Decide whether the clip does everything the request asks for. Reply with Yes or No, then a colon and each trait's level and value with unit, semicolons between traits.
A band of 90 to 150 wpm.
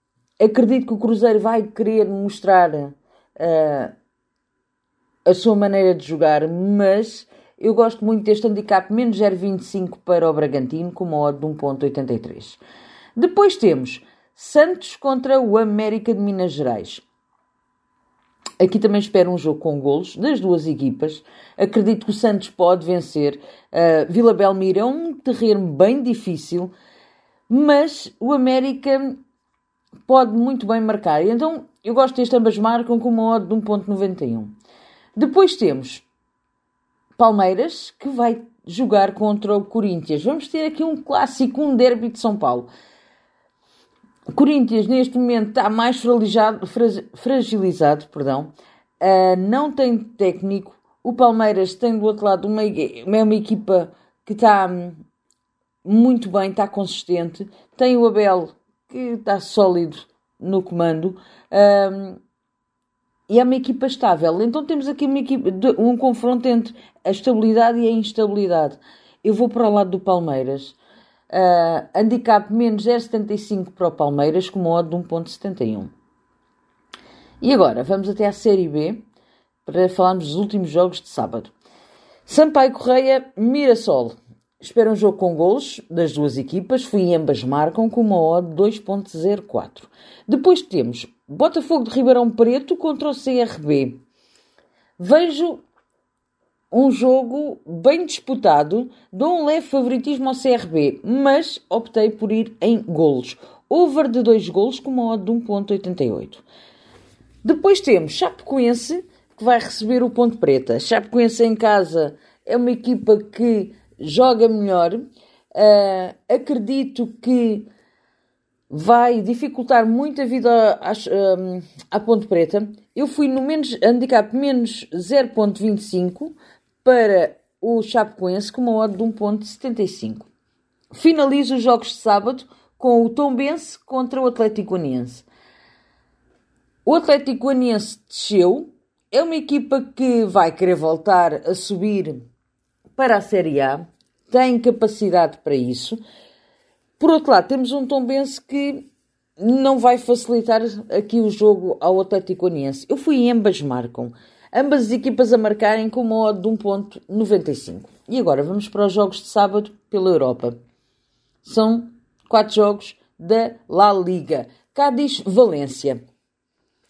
Yes: average, 130 wpm